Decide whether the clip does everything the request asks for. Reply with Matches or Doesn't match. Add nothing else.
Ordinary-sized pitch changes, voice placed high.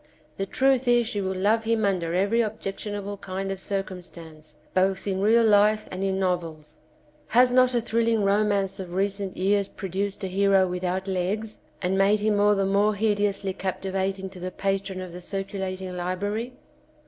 Doesn't match